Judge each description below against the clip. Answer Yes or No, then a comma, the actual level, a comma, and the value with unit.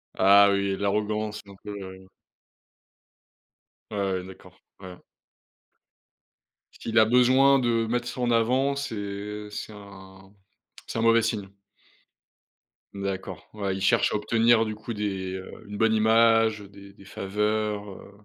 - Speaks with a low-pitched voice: Yes, low, 105 Hz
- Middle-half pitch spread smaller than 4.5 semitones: Yes, narrow, 2.4 semitones